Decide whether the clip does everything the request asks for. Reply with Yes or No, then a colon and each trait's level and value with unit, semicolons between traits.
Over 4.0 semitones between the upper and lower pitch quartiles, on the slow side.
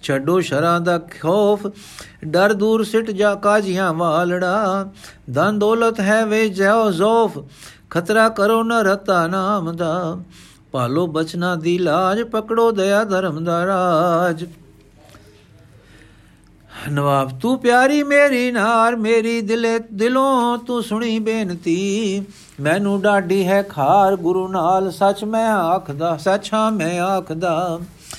No: average, 4.5 semitones; average, 115 wpm